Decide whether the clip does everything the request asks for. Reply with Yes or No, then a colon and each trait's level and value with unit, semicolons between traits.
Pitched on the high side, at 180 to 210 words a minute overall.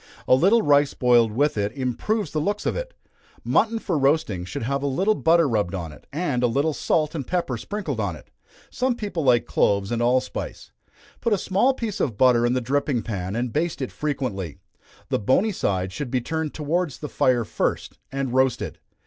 No: low, 135 Hz; average, 200 wpm